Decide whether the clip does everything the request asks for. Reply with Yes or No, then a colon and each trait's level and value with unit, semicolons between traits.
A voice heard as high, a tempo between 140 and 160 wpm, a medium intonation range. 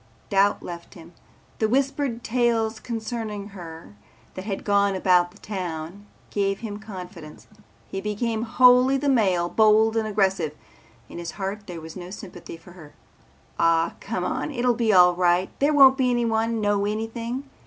Yes: high, 205 Hz; average, 155 wpm; average, 4.3 semitones